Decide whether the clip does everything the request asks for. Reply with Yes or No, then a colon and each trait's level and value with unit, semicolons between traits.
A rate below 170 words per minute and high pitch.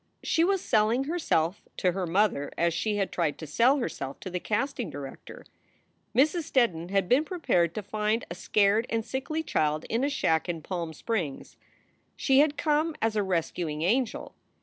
No: average, 175 wpm; high, 210 Hz